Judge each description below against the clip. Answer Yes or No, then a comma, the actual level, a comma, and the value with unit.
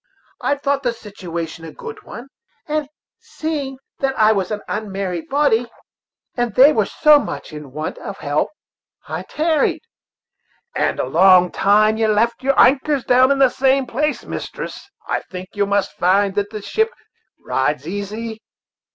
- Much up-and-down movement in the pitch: Yes, wide, 5.9 semitones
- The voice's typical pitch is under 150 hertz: No, high, 220 Hz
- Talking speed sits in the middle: Yes, average, 160 wpm